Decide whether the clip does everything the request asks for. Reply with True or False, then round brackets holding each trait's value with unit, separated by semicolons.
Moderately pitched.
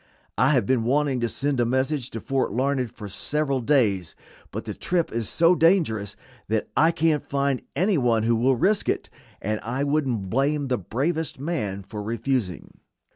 False (130 Hz)